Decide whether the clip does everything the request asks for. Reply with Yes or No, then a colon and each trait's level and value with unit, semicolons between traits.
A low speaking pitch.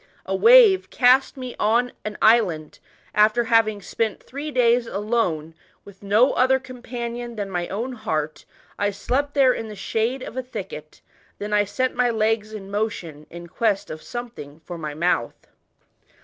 No: high, 220 Hz